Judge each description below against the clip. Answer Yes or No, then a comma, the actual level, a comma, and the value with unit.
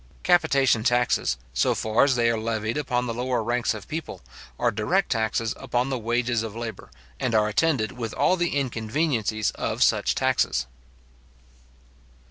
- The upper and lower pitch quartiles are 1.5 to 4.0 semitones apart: Yes, average, 3.0 semitones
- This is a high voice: No, low, 120 Hz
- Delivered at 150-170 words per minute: Yes, average, 155 wpm